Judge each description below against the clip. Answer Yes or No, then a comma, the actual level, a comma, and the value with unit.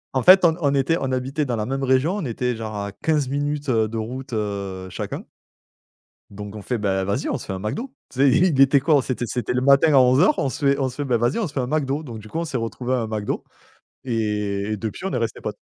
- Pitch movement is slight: No, average, 4.5 semitones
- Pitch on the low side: Yes, low, 130 Hz